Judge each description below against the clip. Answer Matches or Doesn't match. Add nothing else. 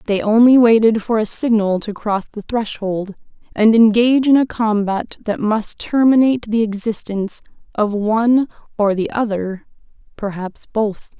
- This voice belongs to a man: Doesn't match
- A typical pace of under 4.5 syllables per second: Doesn't match